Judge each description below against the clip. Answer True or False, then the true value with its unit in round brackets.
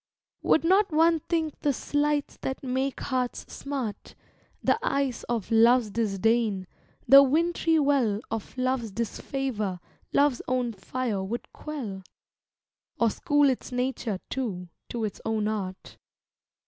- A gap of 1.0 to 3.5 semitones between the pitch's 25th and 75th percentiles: False (4.4 semitones)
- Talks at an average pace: False (125 wpm)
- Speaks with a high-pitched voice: True (250 Hz)